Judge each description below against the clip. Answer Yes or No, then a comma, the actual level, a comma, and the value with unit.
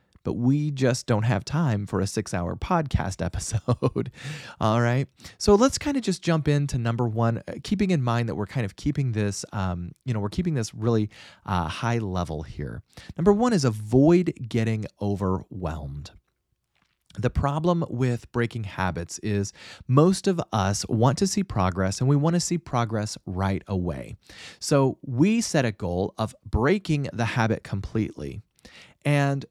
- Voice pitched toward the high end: No, low, 115 Hz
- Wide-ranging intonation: Yes, wide, 6.2 semitones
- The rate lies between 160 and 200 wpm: Yes, average, 165 wpm